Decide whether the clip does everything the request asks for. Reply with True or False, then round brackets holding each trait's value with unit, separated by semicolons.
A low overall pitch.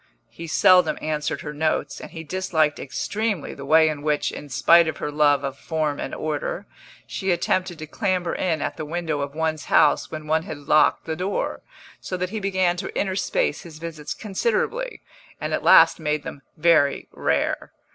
False (160 Hz)